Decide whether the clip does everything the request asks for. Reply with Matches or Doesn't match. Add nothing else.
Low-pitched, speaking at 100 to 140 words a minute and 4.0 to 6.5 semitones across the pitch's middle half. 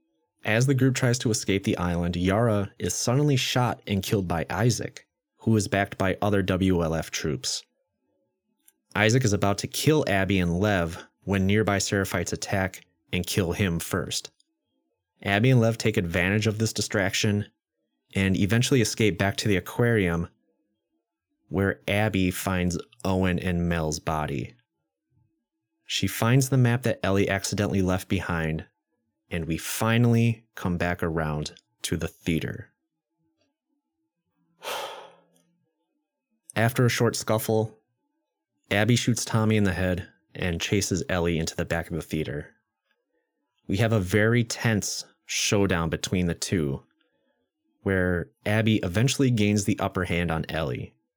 Matches